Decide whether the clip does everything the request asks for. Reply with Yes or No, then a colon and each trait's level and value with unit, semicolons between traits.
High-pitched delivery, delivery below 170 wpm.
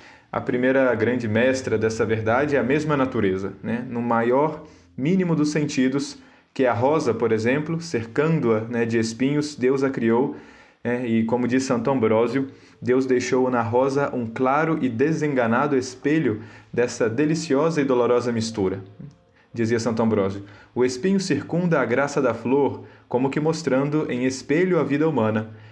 No: low, 125 Hz; average, 155 wpm